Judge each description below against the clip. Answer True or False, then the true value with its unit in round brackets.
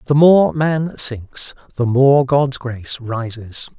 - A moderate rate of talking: True (145 wpm)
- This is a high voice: False (130 Hz)